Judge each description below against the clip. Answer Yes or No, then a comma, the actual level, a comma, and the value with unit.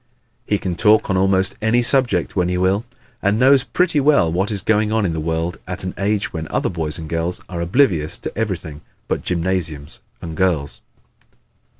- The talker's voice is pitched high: No, very low, 95 Hz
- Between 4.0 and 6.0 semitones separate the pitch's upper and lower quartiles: Yes, average, 4.3 semitones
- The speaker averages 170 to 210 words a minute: Yes, average, 180 wpm